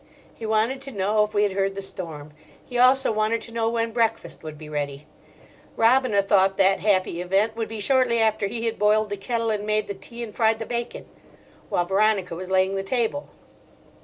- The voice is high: Yes, high, 215 Hz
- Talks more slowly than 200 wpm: No, fast, 205 wpm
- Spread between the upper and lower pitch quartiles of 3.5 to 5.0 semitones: No, average, 3.0 semitones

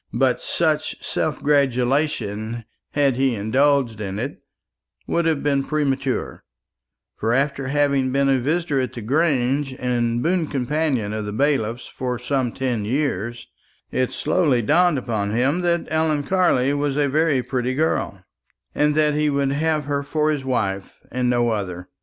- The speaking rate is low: No, average, 155 wpm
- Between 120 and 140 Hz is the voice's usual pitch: Yes, low, 135 Hz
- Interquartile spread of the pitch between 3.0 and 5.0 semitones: Yes, average, 3.6 semitones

